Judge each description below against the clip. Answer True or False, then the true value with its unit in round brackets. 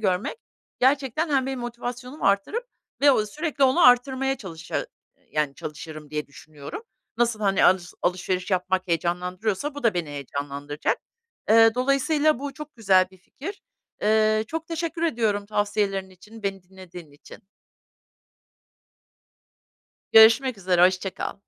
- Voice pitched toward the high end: True (210 Hz)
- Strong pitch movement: True (6.5 semitones)